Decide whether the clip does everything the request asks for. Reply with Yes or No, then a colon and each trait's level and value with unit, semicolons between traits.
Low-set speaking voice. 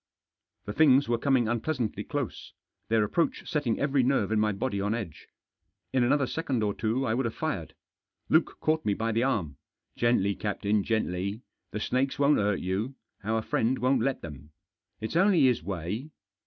Yes: low, 115 Hz